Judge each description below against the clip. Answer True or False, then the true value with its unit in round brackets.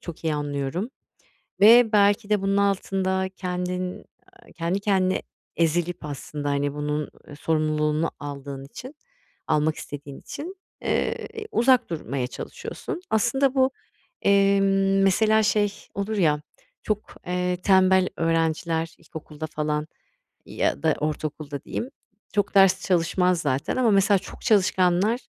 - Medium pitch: True (180 Hz)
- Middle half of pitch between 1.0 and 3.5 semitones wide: False (4.7 semitones)